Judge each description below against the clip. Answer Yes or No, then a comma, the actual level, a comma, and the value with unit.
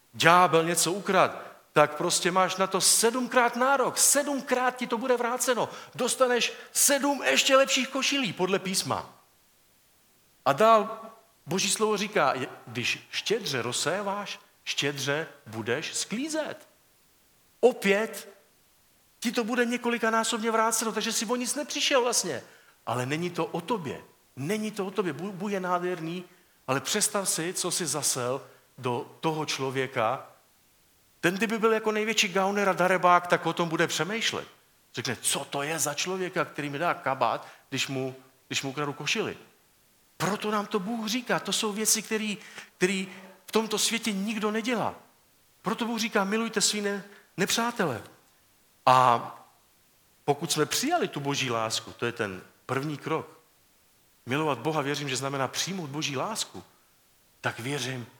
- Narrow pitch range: No, wide, 7.0 semitones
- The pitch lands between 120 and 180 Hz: No, high, 190 Hz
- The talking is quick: No, average, 145 wpm